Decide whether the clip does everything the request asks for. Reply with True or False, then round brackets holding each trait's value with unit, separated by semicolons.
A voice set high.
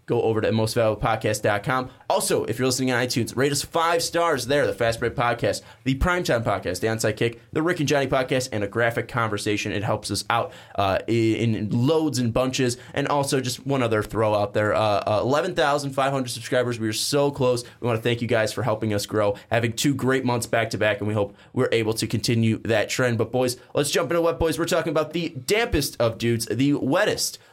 False (120 Hz)